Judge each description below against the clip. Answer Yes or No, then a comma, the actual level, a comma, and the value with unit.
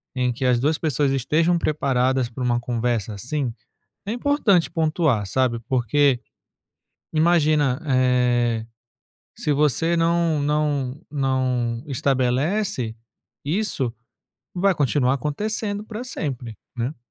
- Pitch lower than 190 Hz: Yes, medium, 140 Hz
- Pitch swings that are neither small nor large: Yes, average, 4.4 semitones